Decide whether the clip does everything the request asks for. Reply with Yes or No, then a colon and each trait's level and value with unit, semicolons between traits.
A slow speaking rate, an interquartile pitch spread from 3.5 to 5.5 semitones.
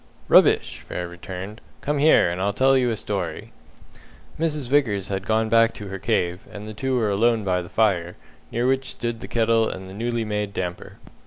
No: average, 195 wpm; average, 3.8 semitones